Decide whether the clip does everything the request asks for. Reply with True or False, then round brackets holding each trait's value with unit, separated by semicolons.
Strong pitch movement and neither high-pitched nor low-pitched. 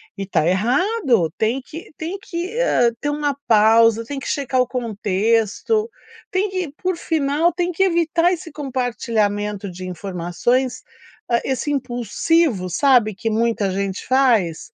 False (7.5 semitones; 245 Hz)